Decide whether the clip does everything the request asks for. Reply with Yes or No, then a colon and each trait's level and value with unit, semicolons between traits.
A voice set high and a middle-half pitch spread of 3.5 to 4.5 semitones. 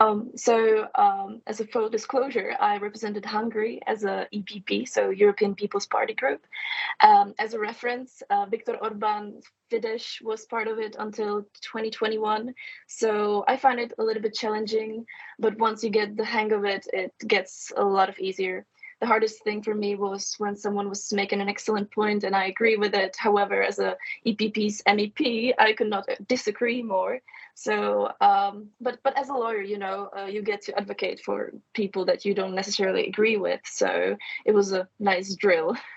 No: high, 215 Hz; average, 3.0 semitones